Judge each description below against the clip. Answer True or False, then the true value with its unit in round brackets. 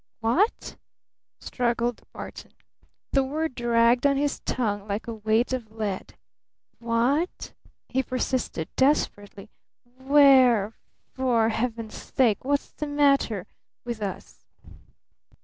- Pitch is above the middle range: True (240 Hz)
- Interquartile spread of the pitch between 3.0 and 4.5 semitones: True (3.4 semitones)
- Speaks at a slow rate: True (120 wpm)